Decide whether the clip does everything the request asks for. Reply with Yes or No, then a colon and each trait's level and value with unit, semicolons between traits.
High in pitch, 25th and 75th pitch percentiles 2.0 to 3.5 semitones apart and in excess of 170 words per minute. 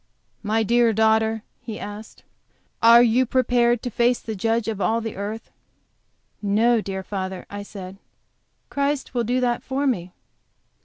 No: high, 225 Hz; average, 2.7 semitones; average, 150 wpm